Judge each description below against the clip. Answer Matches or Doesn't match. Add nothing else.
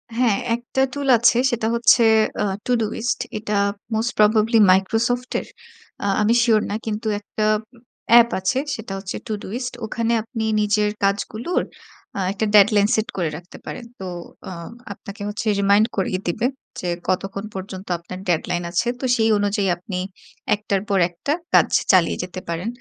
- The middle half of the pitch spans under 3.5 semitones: Matches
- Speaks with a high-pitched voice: Matches